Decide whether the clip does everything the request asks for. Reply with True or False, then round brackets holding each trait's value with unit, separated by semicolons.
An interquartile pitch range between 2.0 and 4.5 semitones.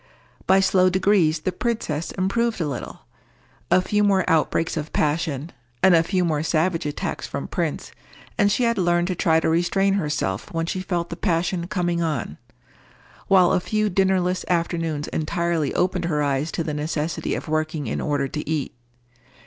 True (3.1 semitones)